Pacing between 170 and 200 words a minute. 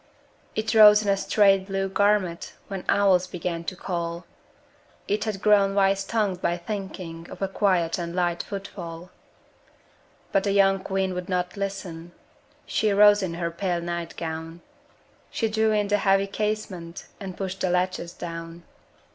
No: average, 155 wpm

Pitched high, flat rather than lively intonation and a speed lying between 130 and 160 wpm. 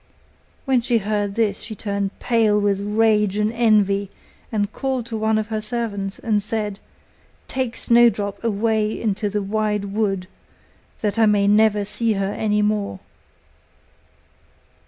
Yes: high, 210 Hz; narrow, 1.7 semitones; average, 140 wpm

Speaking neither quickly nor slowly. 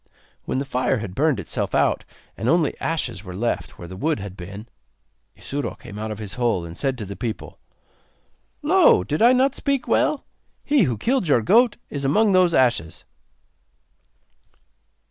Yes: average, 170 wpm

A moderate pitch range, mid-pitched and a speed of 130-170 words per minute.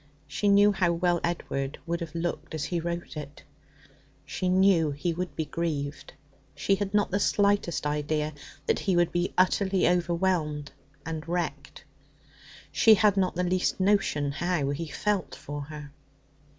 Yes: average, 3.7 semitones; medium, 170 Hz; average, 155 wpm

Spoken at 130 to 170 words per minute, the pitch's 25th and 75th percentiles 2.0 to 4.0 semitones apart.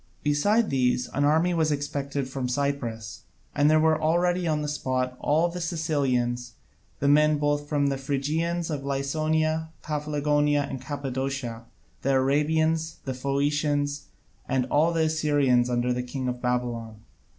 Yes: average, 145 wpm; average, 3.0 semitones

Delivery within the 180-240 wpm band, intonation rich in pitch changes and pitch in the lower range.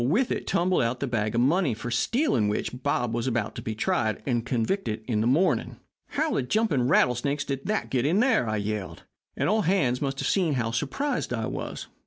Yes: fast, 205 wpm; wide, 7.1 semitones; low, 125 Hz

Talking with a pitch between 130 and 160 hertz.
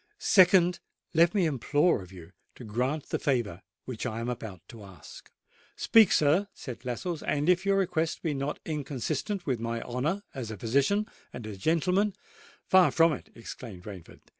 Yes: medium, 140 Hz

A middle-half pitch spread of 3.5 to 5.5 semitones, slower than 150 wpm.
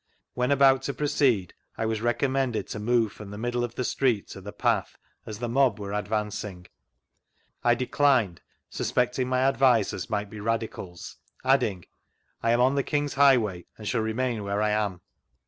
No: average, 3.8 semitones; average, 175 wpm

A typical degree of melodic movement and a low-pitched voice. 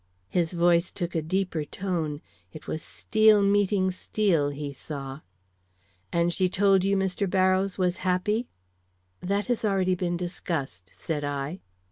No: average, 3.5 semitones; medium, 180 Hz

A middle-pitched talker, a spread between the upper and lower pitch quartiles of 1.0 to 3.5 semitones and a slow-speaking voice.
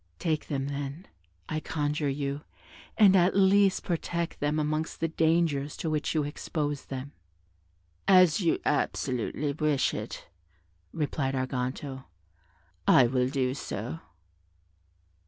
Yes: medium, 150 Hz; average, 3.0 semitones; slow, 120 wpm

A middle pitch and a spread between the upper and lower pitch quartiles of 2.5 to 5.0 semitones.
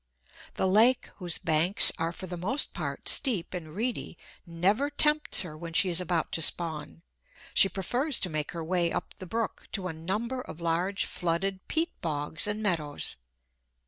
Yes: medium, 180 Hz; average, 4.2 semitones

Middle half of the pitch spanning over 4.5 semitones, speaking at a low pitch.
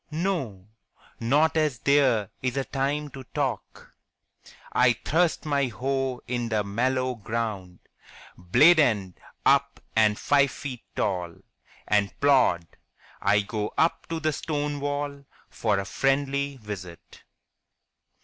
Yes: average, 5.2 semitones; low, 130 Hz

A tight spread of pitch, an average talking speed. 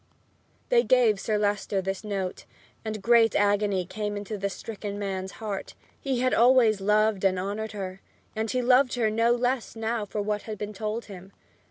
Yes: narrow, 2.3 semitones; average, 180 wpm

